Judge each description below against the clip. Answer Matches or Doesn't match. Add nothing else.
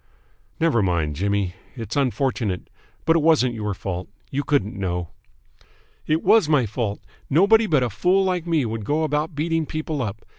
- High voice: Doesn't match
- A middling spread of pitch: Doesn't match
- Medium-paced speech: Matches